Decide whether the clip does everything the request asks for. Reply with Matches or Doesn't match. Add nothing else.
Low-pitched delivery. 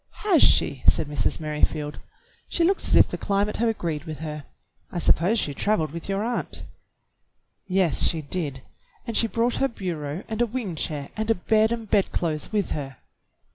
Doesn't match